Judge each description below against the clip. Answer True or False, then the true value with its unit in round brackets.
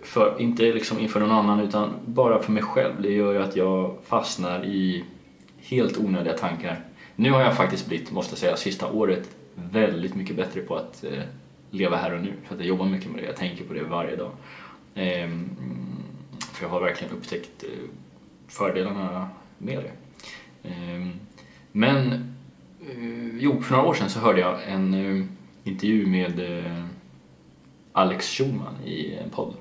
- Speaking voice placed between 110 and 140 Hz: False (95 Hz)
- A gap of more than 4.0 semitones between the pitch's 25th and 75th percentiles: False (3.4 semitones)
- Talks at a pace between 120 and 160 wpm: False (170 wpm)